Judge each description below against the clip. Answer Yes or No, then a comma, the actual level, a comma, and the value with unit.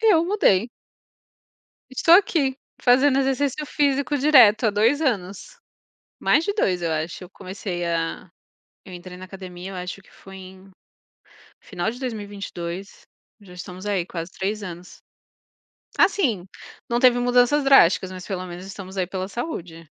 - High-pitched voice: Yes, high, 200 Hz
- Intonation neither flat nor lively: No, wide, 6.5 semitones